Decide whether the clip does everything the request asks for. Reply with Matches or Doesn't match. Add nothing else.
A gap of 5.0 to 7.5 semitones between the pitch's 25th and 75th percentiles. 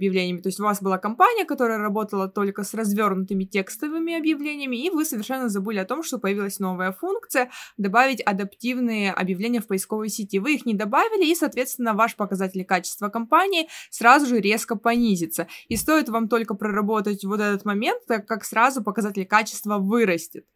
Doesn't match